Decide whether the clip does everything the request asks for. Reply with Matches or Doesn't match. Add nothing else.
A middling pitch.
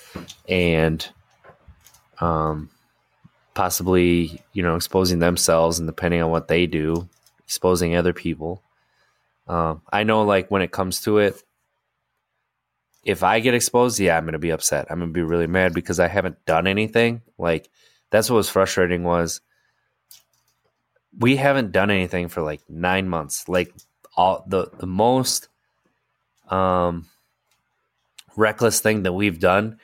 Doesn't match